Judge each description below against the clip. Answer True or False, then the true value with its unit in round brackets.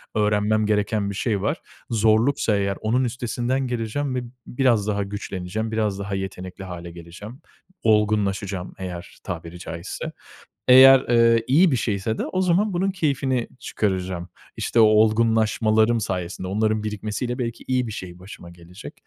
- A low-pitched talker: True (110 Hz)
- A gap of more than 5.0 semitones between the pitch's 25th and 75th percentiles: False (3.8 semitones)